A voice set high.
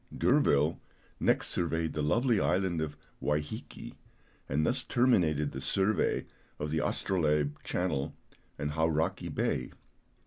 No: very low, 80 Hz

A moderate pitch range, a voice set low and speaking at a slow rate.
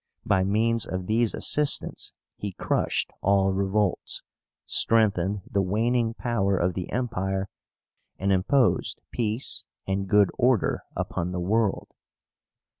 Yes: average, 3.0 semitones; low, 100 Hz; slow, 115 wpm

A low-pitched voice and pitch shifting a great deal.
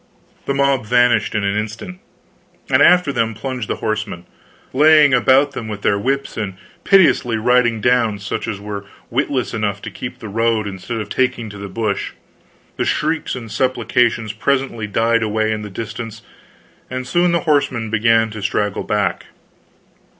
No: low, 115 Hz; average, 3.4 semitones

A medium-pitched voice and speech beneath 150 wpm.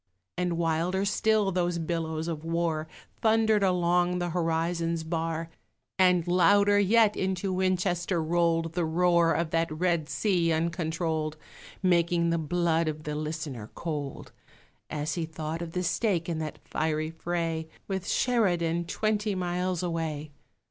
Yes: medium, 170 Hz; slow, 135 wpm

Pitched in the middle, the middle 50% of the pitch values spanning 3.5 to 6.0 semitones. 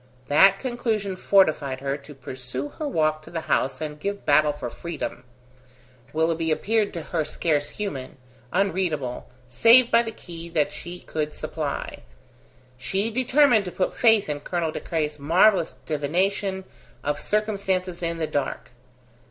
Yes: medium, 165 Hz; average, 5.1 semitones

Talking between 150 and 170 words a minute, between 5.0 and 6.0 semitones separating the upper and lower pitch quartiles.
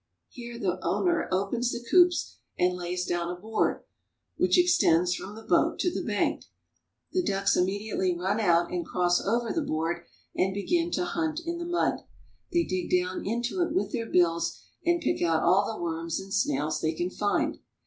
No: average, 190 wpm; wide, 5.6 semitones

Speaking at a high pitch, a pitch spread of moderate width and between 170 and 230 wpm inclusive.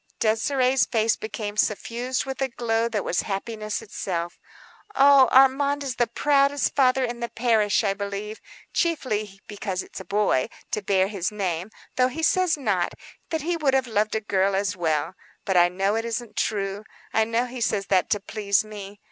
Yes: high, 220 Hz; average, 4.2 semitones; average, 180 wpm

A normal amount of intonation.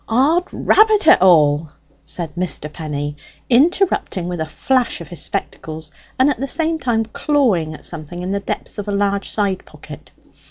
No: wide, 8.5 semitones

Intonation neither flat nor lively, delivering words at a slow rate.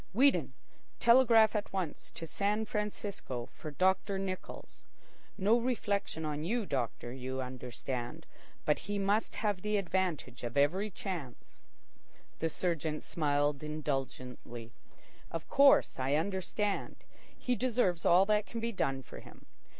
No: wide, 6.7 semitones; slow, 130 wpm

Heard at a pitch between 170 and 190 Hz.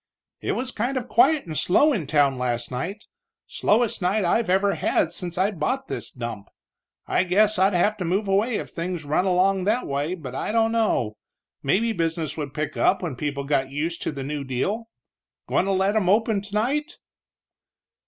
Yes: medium, 185 Hz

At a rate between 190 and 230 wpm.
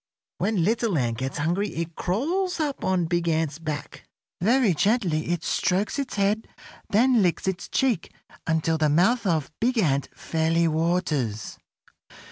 No: average, 145 wpm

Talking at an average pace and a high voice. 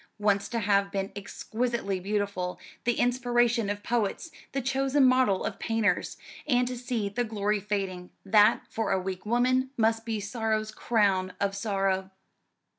Yes: average, 150 wpm; high, 215 Hz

